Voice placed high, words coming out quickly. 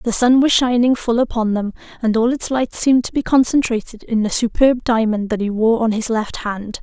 Yes: high, 230 Hz; fast, 230 wpm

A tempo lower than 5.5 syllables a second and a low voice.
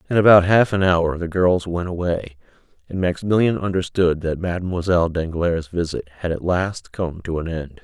Yes: 5.1 syllables/s; very low, 90 Hz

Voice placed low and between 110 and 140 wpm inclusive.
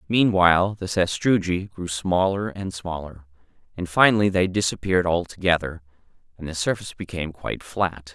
Yes: very low, 90 Hz; slow, 135 wpm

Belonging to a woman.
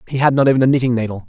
No: male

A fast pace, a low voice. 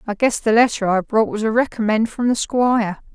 No: fast, 230 wpm; high, 225 Hz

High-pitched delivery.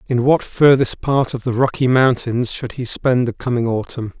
No: low, 125 Hz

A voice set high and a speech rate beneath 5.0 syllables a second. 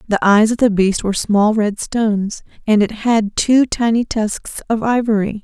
Yes: high, 215 Hz; 4.5 syllables/s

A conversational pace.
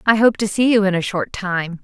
No: fast, 295 wpm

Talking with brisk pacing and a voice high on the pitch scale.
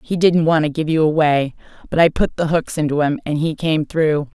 No: fast, 245 wpm; medium, 155 Hz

